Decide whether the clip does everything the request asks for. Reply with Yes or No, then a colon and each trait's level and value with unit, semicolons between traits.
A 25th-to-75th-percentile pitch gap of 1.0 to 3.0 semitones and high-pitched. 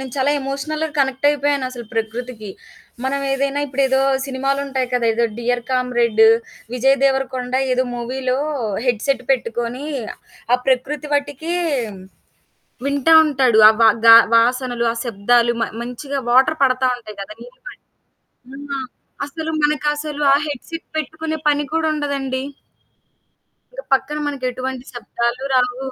Yes: average, 2.7 semitones; very high, 260 Hz